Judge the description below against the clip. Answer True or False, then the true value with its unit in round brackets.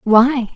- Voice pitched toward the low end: False (240 Hz)